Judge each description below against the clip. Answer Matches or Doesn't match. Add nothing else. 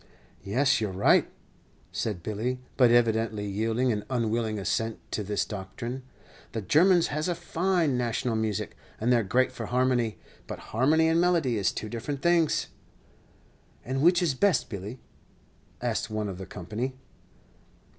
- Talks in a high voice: Doesn't match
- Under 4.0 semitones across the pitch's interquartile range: Doesn't match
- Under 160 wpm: Matches